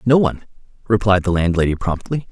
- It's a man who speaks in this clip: Yes, male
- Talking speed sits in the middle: Yes, average, 155 wpm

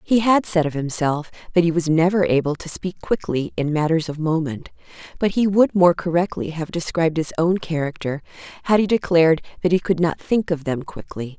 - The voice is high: No, medium, 165 Hz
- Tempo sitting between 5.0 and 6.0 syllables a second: Yes, 5.4 syllables/s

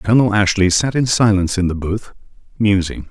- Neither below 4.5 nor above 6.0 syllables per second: Yes, 5.7 syllables/s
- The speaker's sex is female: No, male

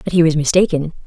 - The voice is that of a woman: Yes, female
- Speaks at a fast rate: Yes, fast, 225 wpm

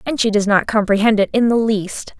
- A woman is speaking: Yes, female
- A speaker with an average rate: No, fast, 245 wpm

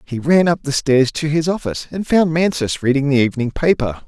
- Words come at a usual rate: No, fast, 220 wpm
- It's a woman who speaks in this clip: No, male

